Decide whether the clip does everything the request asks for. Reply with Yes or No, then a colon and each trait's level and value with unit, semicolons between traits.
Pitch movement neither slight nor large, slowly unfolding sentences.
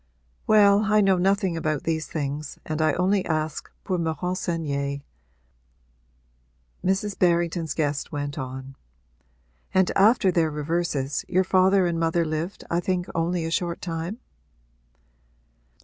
Yes: average, 3.2 semitones; slow, 130 wpm